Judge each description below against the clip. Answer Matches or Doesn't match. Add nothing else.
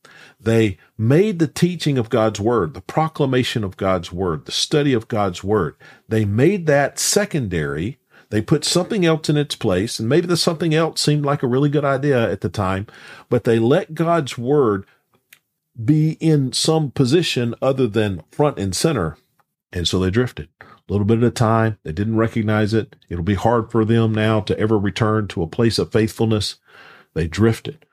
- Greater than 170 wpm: Matches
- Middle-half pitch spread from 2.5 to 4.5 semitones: Doesn't match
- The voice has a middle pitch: Doesn't match